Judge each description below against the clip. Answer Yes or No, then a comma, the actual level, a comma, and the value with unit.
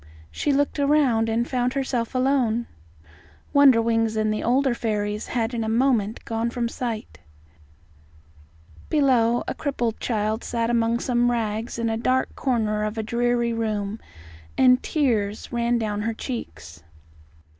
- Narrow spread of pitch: Yes, narrow, 2.3 semitones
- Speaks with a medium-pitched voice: No, high, 230 Hz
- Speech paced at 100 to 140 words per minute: Yes, slow, 135 wpm